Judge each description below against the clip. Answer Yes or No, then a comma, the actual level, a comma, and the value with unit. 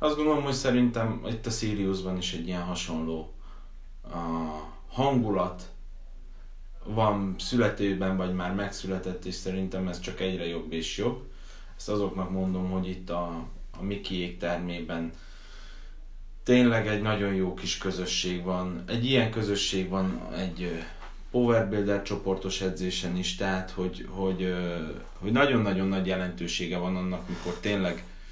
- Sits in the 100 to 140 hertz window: No, very low, 90 Hz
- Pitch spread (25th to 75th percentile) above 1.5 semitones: Yes, average, 2.7 semitones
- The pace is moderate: Yes, average, 135 wpm